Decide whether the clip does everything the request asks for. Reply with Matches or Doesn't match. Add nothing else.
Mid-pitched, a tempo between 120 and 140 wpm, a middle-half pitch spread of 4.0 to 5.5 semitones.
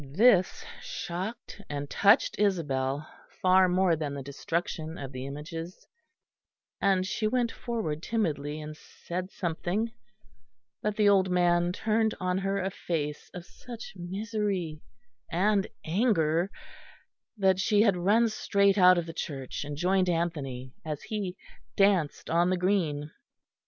Matches